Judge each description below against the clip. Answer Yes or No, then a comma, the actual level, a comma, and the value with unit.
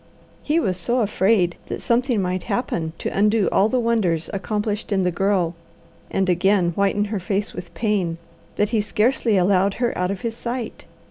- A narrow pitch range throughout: No, average, 3.6 semitones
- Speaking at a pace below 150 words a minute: No, average, 180 wpm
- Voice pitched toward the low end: No, high, 200 Hz